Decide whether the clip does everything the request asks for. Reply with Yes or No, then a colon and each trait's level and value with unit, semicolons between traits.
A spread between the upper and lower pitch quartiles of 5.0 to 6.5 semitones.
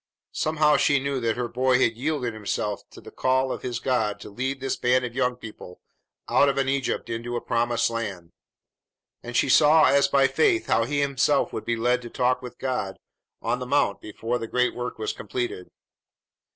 No: average, 2.8 semitones